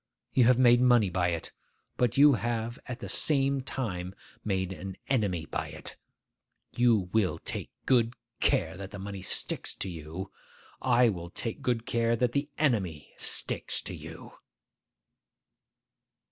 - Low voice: Yes, low, 115 Hz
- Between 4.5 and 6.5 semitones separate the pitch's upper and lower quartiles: Yes, average, 4.9 semitones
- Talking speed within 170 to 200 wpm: No, average, 145 wpm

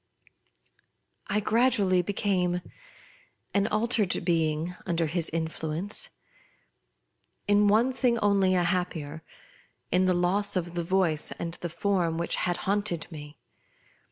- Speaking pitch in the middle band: Yes, medium, 180 Hz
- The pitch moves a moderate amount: Yes, average, 3.4 semitones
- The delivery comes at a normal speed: No, slow, 125 wpm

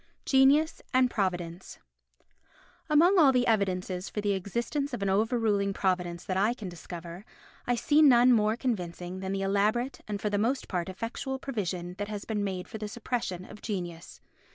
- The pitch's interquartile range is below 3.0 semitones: No, average, 4.6 semitones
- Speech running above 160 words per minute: Yes, average, 175 wpm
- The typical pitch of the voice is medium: No, high, 205 Hz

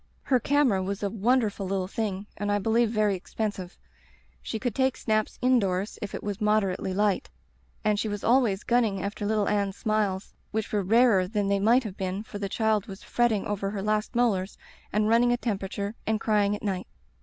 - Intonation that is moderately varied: No, narrow, 2.1 semitones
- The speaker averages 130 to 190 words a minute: No, average, 200 wpm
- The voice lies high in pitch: Yes, high, 210 Hz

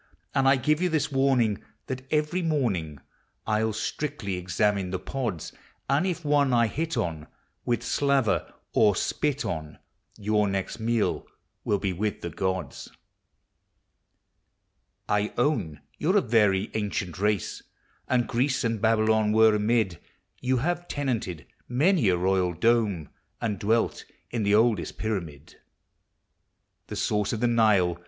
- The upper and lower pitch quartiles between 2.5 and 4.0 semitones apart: No, wide, 5.4 semitones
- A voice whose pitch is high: No, low, 110 Hz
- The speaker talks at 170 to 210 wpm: No, average, 140 wpm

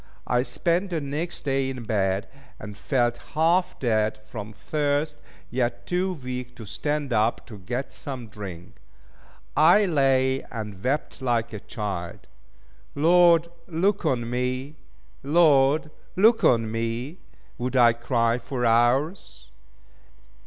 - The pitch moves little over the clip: No, average, 4.8 semitones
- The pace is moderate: No, slow, 125 wpm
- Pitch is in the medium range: No, low, 130 Hz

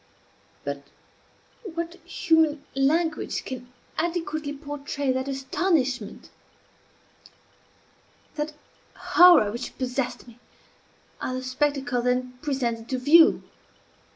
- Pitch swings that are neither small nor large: Yes, average, 3.8 semitones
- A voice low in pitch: No, very high, 275 Hz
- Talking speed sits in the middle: No, slow, 90 wpm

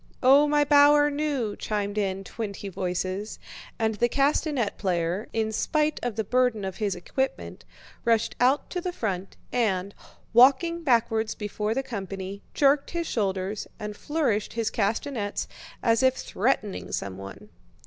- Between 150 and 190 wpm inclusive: No, average, 140 wpm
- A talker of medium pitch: No, high, 220 Hz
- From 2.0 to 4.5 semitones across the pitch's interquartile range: No, wide, 5.4 semitones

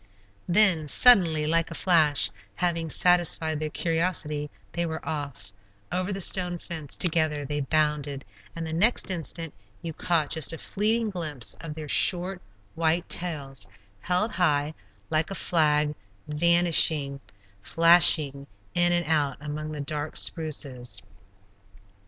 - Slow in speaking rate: Yes, slow, 130 wpm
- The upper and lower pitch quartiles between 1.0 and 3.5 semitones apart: Yes, average, 2.8 semitones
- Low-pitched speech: No, medium, 160 Hz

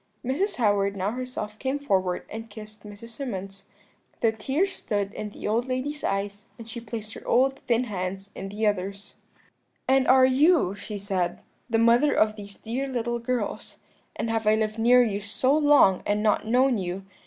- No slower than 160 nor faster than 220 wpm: Yes, average, 180 wpm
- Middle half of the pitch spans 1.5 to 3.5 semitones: No, average, 3.9 semitones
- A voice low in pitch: No, high, 220 Hz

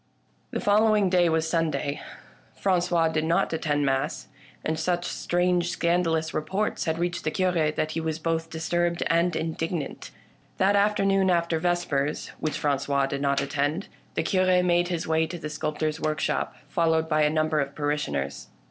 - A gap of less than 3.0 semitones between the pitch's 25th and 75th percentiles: Yes, narrow, 2.4 semitones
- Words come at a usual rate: Yes, average, 165 wpm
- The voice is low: No, medium, 160 Hz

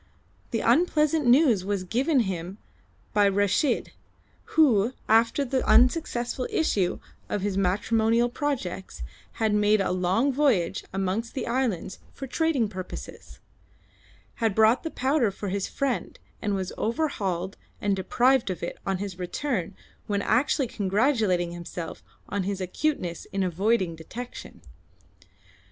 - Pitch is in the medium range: No, high, 215 Hz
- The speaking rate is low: Yes, slow, 130 wpm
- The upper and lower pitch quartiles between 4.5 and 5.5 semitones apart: Yes, average, 5.2 semitones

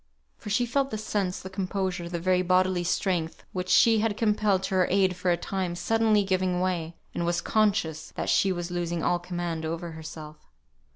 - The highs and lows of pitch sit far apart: No, narrow, 2.4 semitones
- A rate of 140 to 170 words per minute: No, average, 190 wpm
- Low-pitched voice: No, medium, 185 Hz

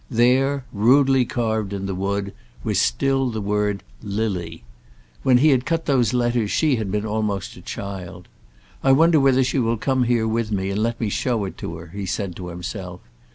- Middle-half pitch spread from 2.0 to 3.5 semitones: No, average, 4.4 semitones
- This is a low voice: Yes, low, 110 Hz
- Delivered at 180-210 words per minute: Yes, average, 190 wpm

